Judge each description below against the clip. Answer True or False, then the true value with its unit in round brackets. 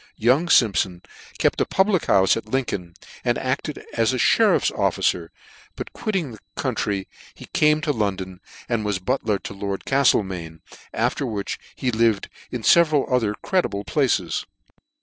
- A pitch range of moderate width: False (5.9 semitones)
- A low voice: True (115 Hz)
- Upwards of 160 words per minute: False (150 wpm)